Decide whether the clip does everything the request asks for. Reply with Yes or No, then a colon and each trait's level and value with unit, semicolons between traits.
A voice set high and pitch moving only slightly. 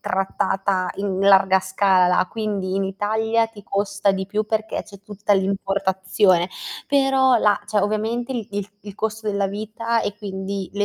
Yes: high, 200 Hz; narrow, 2.1 semitones